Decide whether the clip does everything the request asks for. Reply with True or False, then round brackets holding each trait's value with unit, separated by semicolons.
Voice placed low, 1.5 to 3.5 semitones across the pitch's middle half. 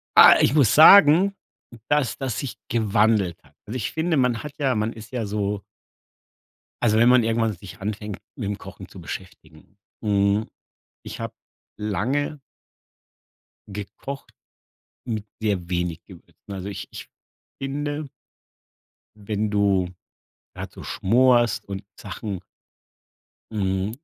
False (110 Hz; 4.1 semitones)